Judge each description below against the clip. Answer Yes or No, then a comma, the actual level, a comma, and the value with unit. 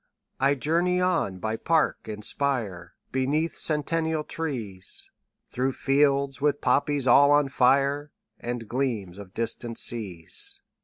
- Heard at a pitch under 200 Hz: Yes, low, 135 Hz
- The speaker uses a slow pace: Yes, slow, 125 wpm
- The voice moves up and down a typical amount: Yes, average, 4.5 semitones